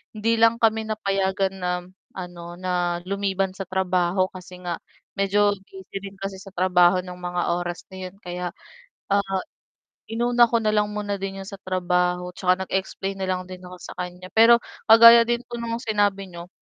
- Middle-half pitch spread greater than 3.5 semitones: No, narrow, 2.4 semitones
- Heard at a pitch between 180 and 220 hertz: Yes, high, 190 Hz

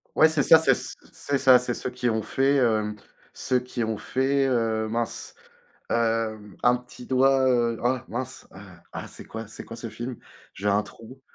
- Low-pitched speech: Yes, low, 120 Hz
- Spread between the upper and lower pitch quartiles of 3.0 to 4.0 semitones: No, narrow, 2.6 semitones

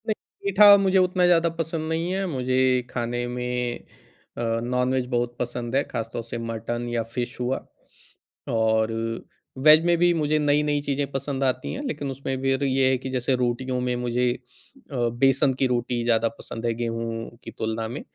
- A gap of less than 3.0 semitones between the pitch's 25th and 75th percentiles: No, average, 3.5 semitones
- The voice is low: Yes, low, 130 Hz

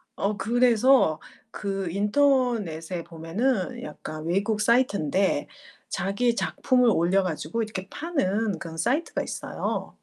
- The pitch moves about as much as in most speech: No, wide, 5.9 semitones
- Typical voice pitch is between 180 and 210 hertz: Yes, high, 200 Hz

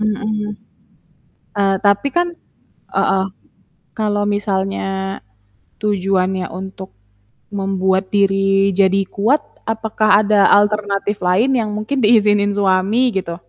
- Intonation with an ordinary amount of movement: No, narrow, 1.7 semitones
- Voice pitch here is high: Yes, high, 200 Hz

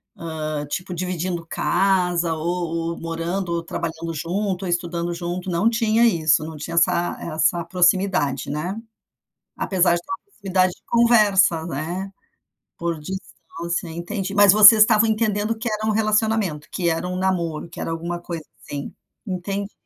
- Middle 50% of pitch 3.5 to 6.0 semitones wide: No, average, 3.0 semitones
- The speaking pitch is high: No, medium, 175 Hz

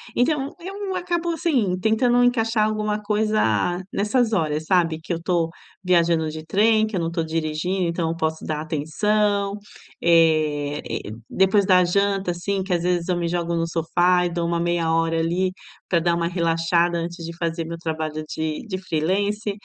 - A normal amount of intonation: Yes, average, 3.9 semitones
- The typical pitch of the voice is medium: Yes, medium, 175 Hz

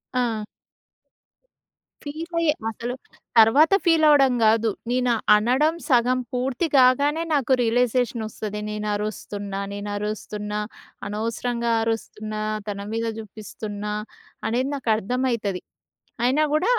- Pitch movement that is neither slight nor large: Yes, average, 3.6 semitones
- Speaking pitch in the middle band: No, high, 235 Hz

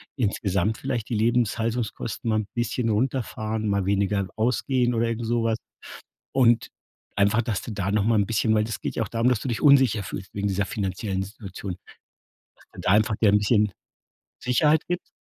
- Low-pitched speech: Yes, low, 110 Hz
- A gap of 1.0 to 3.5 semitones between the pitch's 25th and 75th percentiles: Yes, average, 2.7 semitones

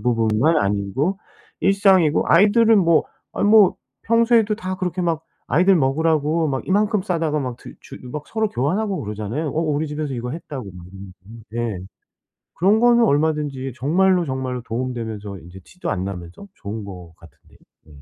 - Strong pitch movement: Yes, wide, 8.6 semitones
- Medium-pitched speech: Yes, medium, 150 Hz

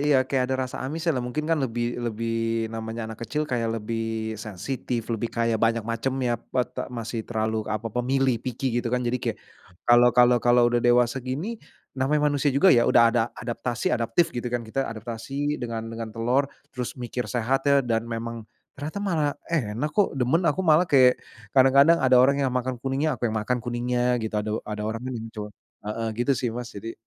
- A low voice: Yes, low, 120 Hz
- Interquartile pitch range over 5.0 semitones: No, average, 2.7 semitones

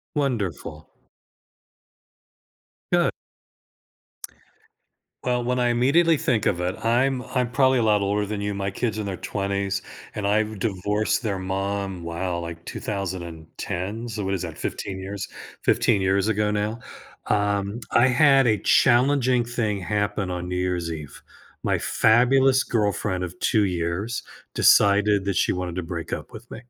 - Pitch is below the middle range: Yes, low, 100 Hz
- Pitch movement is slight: No, average, 4.1 semitones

